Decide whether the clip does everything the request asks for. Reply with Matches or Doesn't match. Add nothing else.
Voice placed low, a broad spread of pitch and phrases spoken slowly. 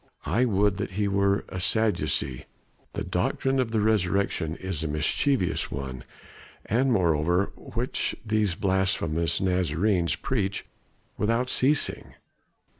Doesn't match